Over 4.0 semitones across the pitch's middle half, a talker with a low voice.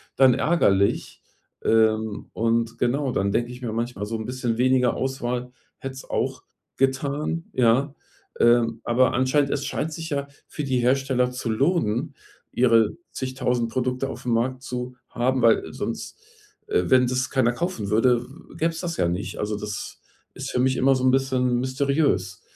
No: narrow, 2.4 semitones; low, 125 Hz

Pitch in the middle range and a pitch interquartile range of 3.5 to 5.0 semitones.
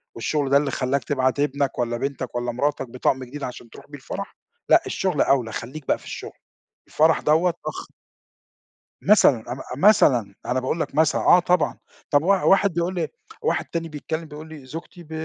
Yes: medium, 145 Hz; average, 4.1 semitones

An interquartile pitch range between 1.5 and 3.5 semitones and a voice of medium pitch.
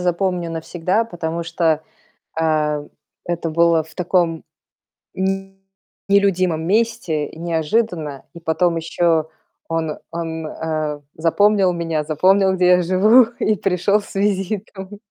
Yes: average, 3.1 semitones; medium, 170 Hz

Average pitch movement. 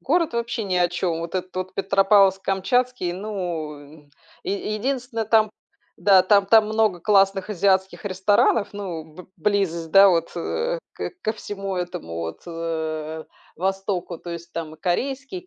Yes: average, 3.7 semitones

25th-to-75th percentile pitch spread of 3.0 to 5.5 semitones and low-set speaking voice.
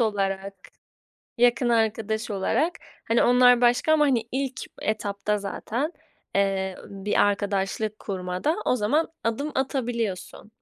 No: average, 3.8 semitones; high, 220 Hz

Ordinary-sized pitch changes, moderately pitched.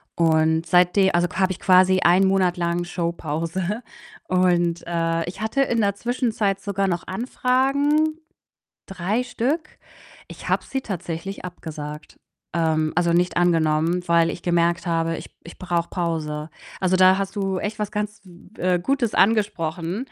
Yes: average, 3.2 semitones; medium, 180 Hz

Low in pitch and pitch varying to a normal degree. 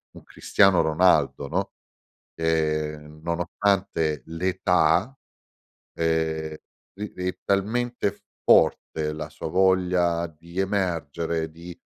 Yes: very low, 85 Hz; average, 3.0 semitones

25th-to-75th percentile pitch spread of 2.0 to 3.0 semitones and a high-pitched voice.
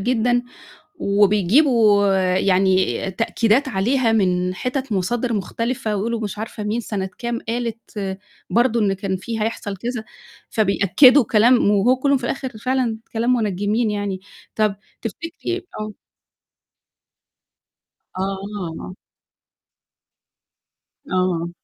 No: average, 3.6 semitones; high, 215 Hz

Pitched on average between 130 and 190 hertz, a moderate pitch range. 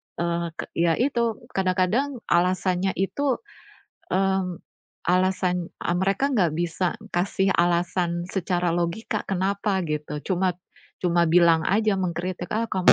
No: medium, 185 Hz; narrow, 2.0 semitones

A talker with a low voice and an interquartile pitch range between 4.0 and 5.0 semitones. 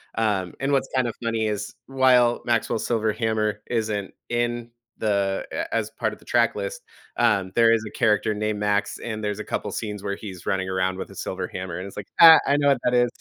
No: low, 110 Hz; average, 2.7 semitones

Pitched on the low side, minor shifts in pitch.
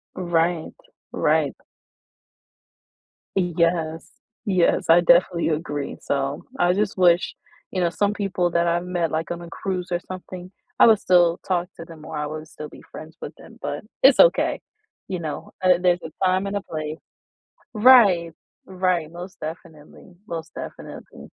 No: medium, 175 Hz; narrow, 2.1 semitones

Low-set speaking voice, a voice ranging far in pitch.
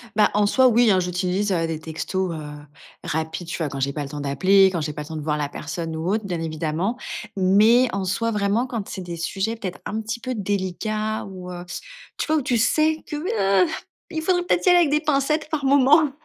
No: high, 195 Hz; wide, 6.4 semitones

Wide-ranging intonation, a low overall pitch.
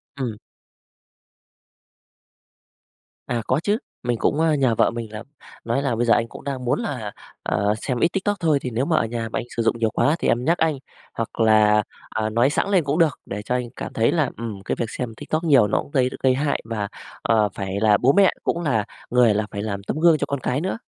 No: average, 4.6 semitones; low, 120 Hz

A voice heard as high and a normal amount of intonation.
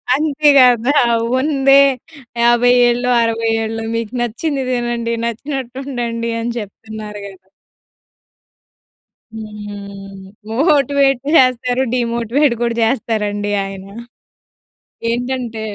Yes: high, 235 Hz; average, 3.0 semitones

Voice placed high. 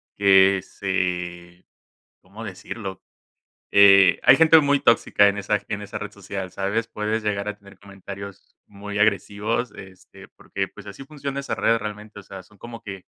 No: low, 100 Hz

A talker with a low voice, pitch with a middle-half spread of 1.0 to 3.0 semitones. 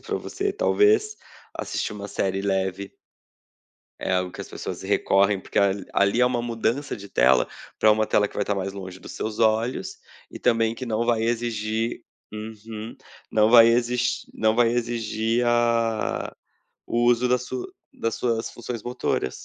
Yes: low, 115 Hz; narrow, 2.4 semitones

